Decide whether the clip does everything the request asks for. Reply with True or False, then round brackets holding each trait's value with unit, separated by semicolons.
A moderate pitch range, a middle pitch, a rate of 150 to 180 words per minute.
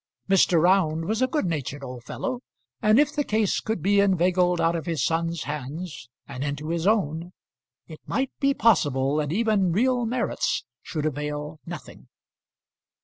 False (5.9 semitones; 170 Hz; 160 wpm)